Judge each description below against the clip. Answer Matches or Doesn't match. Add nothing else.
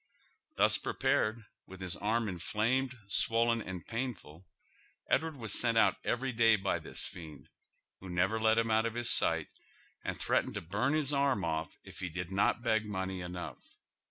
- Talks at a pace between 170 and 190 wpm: Matches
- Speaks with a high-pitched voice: Doesn't match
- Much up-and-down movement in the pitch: Doesn't match